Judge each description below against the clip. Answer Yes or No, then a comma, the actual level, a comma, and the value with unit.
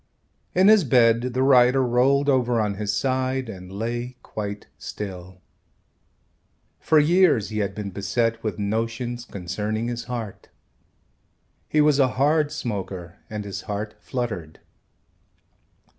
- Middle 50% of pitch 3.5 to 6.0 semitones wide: Yes, average, 4.0 semitones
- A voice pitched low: Yes, low, 115 Hz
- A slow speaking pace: Yes, slow, 130 wpm